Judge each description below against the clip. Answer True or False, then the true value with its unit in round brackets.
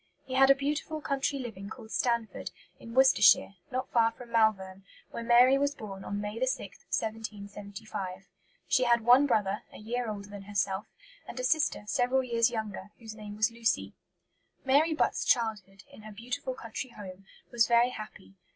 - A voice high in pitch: True (230 Hz)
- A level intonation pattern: False (3.6 semitones)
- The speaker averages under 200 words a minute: True (170 wpm)